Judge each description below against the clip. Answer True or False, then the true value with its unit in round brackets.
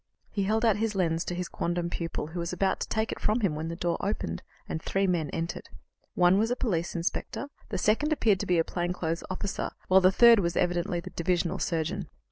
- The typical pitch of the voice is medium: True (180 Hz)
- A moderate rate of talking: False (230 wpm)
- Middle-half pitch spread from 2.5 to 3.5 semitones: True (3.1 semitones)